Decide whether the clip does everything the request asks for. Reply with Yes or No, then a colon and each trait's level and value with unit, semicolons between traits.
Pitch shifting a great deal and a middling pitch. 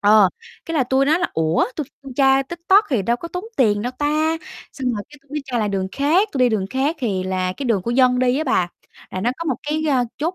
No: wide, 5.8 semitones; very high, 260 Hz